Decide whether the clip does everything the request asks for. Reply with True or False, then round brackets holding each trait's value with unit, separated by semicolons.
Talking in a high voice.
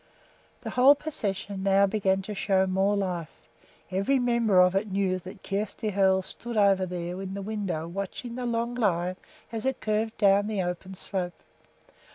True (195 Hz)